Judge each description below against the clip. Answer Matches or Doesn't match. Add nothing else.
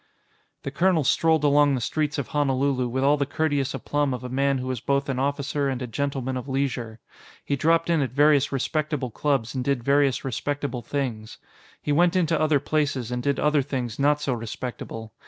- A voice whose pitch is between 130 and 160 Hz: Matches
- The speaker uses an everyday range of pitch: Doesn't match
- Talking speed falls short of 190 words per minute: Doesn't match